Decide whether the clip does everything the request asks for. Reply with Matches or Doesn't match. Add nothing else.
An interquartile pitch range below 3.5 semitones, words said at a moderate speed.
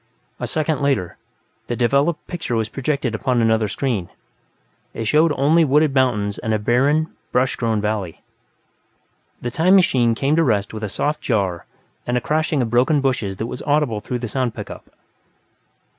Doesn't match